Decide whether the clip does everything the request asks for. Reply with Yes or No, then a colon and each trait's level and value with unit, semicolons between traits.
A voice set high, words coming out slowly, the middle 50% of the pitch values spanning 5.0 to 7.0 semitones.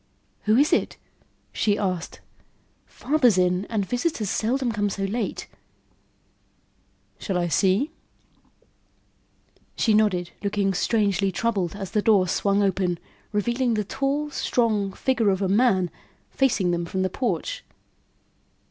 No: high, 205 Hz; slow, 125 wpm; average, 3.7 semitones